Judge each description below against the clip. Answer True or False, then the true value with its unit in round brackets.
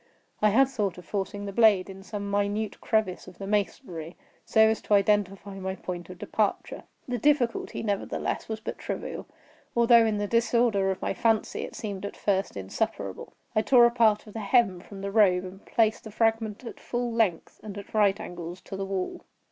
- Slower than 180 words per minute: False (195 wpm)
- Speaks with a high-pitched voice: True (205 Hz)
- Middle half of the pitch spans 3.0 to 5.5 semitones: False (2.5 semitones)